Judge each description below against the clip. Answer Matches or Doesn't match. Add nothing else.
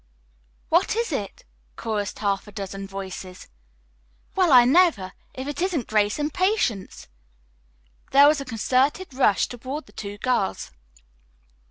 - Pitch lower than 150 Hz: Doesn't match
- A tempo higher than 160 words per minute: Doesn't match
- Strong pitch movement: Matches